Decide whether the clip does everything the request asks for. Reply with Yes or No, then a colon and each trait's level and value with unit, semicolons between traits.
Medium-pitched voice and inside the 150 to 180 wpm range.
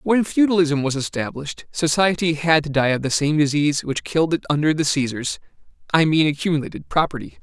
Yes: medium, 150 Hz; average, 170 wpm